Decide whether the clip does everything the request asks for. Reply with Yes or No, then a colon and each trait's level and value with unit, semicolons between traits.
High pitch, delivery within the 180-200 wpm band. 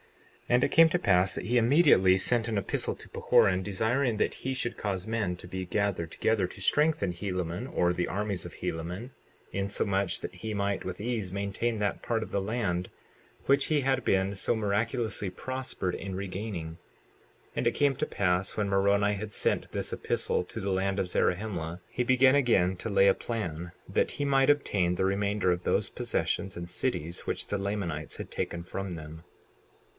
No: low, 100 Hz; average, 190 wpm